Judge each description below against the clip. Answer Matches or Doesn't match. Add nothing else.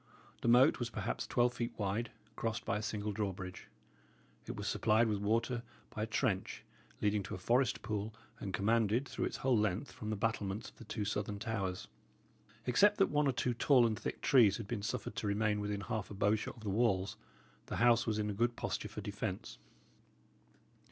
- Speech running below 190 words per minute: Doesn't match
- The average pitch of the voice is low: Matches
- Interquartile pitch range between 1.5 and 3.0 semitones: Matches